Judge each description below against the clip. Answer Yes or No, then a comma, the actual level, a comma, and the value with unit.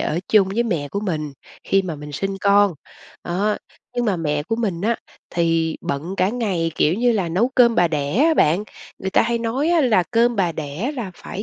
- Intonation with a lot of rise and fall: Yes, wide, 5.7 semitones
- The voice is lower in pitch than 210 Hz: Yes, high, 195 Hz